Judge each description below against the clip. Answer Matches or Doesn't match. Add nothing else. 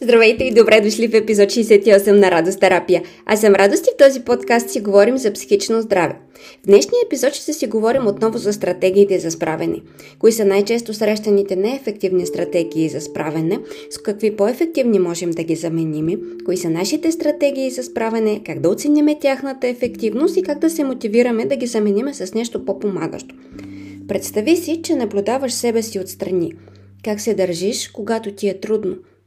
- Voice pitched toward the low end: Doesn't match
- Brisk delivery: Matches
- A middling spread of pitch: Matches